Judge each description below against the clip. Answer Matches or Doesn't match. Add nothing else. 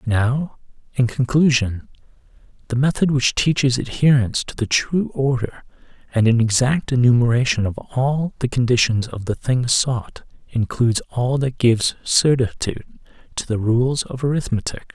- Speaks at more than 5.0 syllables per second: Doesn't match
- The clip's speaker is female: Doesn't match